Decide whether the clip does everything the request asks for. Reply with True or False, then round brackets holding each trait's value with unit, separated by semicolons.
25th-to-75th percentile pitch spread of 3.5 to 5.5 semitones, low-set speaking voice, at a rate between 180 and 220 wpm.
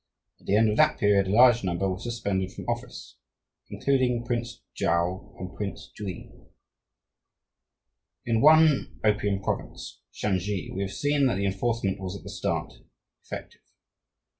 False (3.8 semitones; 105 Hz; 145 wpm)